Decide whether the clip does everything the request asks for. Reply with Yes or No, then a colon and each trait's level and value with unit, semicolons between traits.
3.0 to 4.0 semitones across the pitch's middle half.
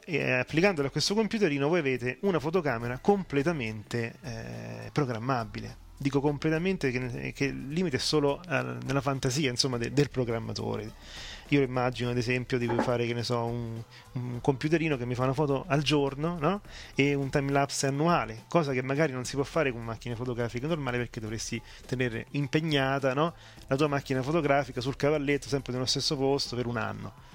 Yes: average, 3.3 semitones